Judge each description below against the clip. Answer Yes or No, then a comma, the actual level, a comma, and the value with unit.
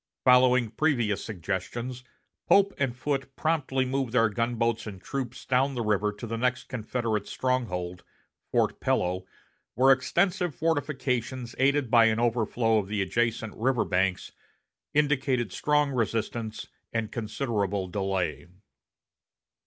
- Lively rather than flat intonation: No, average, 3.7 semitones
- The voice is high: No, low, 120 Hz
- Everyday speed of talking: No, slow, 120 wpm